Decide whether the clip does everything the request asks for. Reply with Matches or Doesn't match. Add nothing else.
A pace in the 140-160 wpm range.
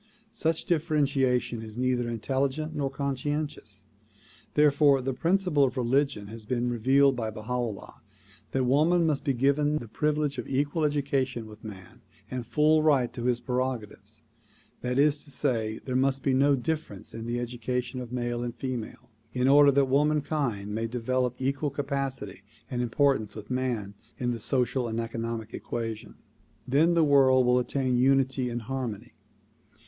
Matches